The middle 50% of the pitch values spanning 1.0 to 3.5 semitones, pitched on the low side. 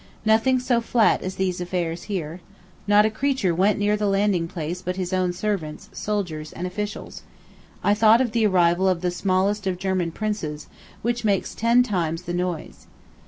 No: average, 3.1 semitones; high, 190 Hz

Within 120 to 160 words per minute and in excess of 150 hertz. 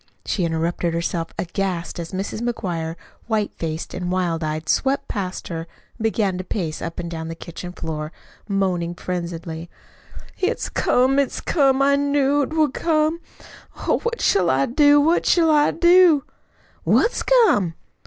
Yes: average, 155 wpm; high, 190 Hz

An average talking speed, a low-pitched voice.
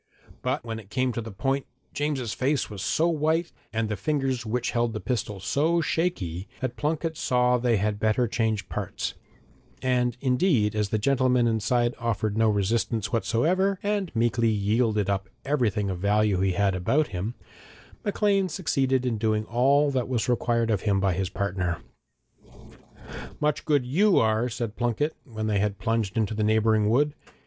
Yes: average, 170 wpm; low, 115 Hz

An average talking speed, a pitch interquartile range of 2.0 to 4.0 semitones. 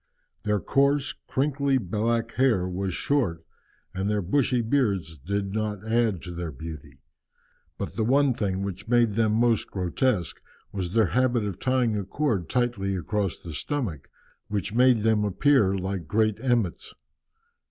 No: average, 150 wpm; average, 4.5 semitones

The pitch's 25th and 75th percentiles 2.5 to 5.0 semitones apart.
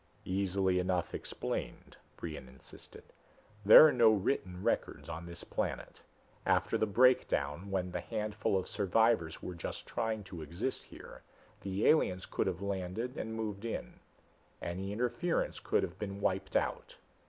Yes: average, 3.5 semitones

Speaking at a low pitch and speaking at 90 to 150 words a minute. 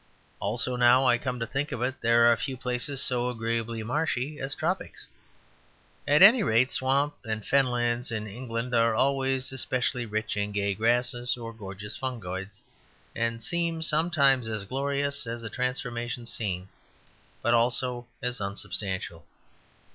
Yes: low, 120 Hz; average, 145 wpm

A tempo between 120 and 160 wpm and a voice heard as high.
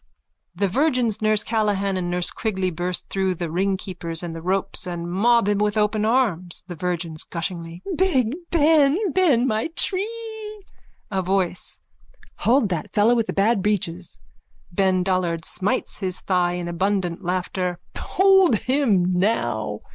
Yes: average, 145 wpm; high, 195 Hz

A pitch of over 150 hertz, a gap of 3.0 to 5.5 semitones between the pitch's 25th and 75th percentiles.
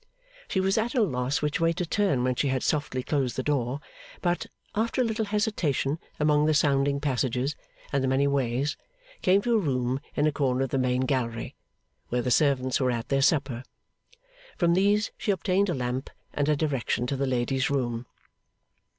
No: medium, 140 Hz; average, 4.5 semitones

